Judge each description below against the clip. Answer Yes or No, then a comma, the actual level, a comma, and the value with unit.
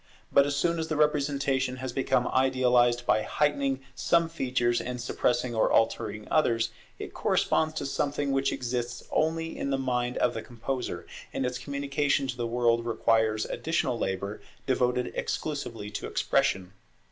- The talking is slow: No, average, 155 wpm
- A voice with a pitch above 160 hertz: No, low, 125 Hz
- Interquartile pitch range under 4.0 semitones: Yes, average, 2.9 semitones